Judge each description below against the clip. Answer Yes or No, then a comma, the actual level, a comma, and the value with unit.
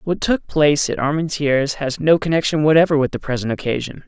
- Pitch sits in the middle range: Yes, medium, 150 Hz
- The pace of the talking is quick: No, average, 190 wpm